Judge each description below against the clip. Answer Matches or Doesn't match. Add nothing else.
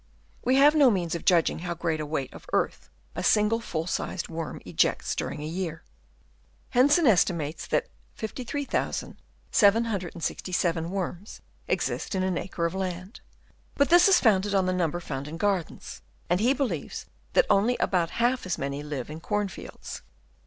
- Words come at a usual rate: Matches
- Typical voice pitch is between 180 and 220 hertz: Matches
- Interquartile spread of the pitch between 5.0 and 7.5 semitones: Matches